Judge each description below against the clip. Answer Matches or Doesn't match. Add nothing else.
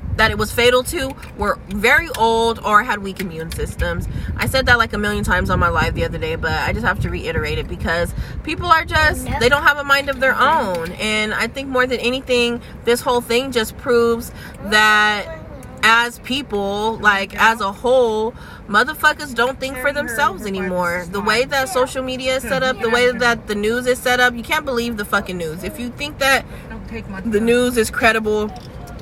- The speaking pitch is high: Matches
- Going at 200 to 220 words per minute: Matches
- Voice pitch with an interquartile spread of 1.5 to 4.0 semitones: Matches